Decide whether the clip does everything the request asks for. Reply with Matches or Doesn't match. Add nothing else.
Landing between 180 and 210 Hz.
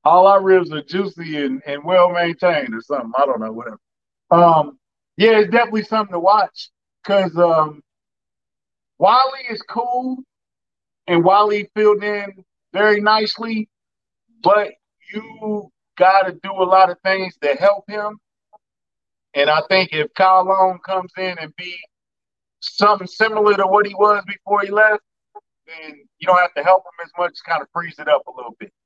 Matches